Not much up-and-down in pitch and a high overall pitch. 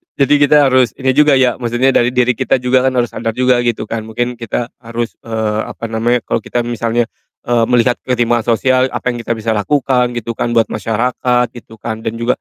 No: narrow, 1.7 semitones; low, 120 Hz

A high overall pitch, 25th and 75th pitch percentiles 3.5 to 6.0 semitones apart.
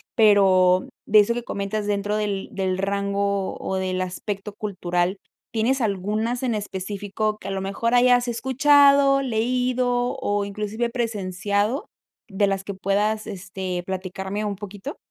No: high, 205 Hz; average, 3.1 semitones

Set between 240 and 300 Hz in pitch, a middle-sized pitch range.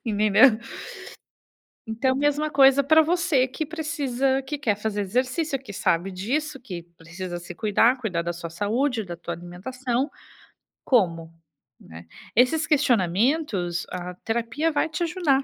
No: high, 245 Hz; wide, 7.3 semitones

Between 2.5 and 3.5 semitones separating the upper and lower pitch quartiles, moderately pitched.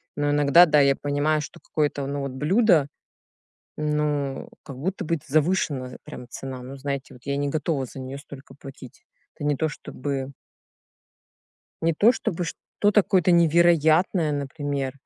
Yes: average, 2.8 semitones; medium, 145 Hz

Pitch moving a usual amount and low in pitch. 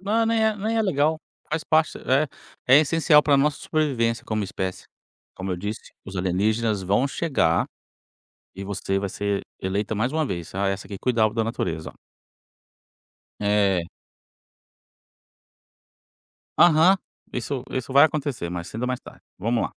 No: wide, 7.5 semitones; low, 115 Hz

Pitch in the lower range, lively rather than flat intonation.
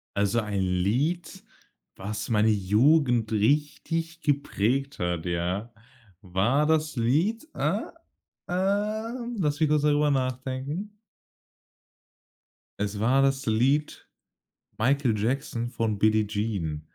Yes: low, 130 Hz; wide, 6.2 semitones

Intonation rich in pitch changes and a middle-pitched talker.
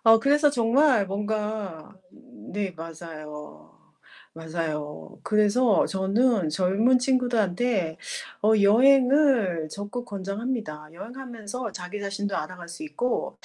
No: wide, 5.8 semitones; high, 205 Hz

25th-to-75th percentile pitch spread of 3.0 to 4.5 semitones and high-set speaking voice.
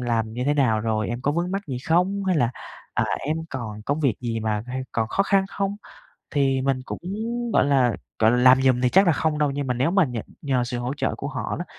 No: average, 4.1 semitones; low, 130 Hz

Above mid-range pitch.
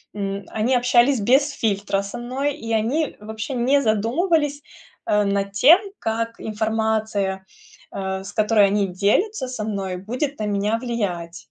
Yes: high, 220 Hz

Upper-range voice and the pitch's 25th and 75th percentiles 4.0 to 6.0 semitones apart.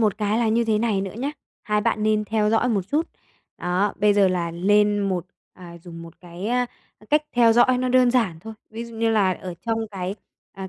No: high, 210 Hz; average, 3.5 semitones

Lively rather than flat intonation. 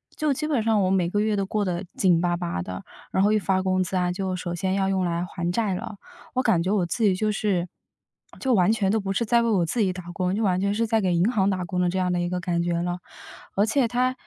No: average, 3.2 semitones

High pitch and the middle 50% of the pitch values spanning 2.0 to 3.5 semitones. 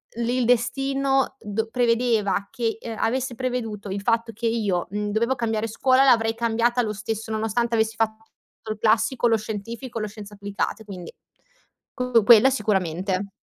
Yes: high, 225 Hz; narrow, 2.4 semitones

